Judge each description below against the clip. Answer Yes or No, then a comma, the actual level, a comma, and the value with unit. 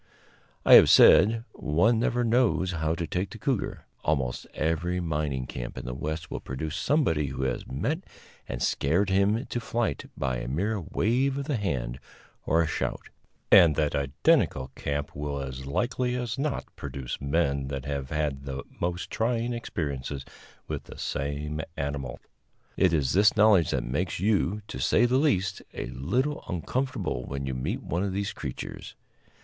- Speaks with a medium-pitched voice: No, very low, 80 Hz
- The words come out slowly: No, average, 165 wpm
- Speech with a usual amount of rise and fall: No, wide, 7.8 semitones